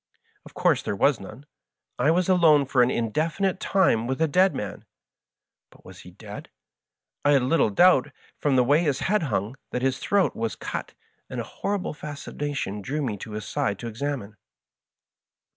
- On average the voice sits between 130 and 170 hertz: Yes, medium, 140 Hz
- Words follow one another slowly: No, average, 180 wpm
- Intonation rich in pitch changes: Yes, wide, 5.7 semitones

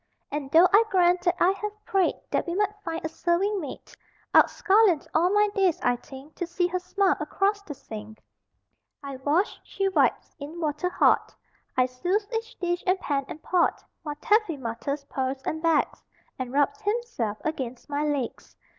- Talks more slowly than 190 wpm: Yes, average, 180 wpm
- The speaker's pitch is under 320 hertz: No, very high, 340 Hz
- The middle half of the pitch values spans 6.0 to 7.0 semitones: No, wide, 5.5 semitones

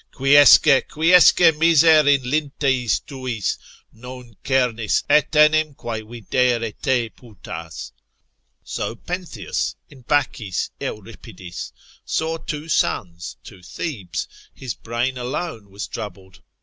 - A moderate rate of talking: No, slow, 100 wpm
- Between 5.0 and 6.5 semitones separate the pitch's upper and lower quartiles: Yes, average, 5.3 semitones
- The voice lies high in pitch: No, low, 125 Hz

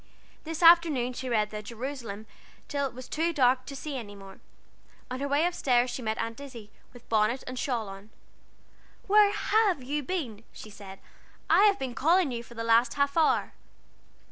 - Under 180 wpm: No, average, 190 wpm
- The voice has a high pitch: Yes, very high, 255 Hz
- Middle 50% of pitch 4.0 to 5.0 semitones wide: Yes, average, 4.7 semitones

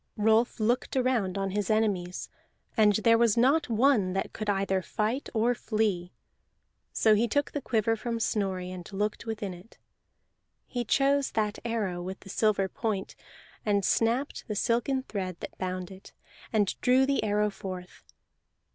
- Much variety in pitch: No, average, 3.3 semitones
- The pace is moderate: Yes, average, 155 wpm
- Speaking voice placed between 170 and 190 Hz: No, high, 215 Hz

